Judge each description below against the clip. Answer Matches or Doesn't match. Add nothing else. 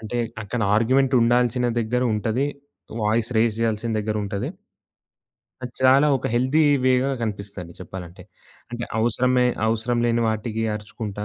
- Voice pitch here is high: Doesn't match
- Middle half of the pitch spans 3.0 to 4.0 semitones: Doesn't match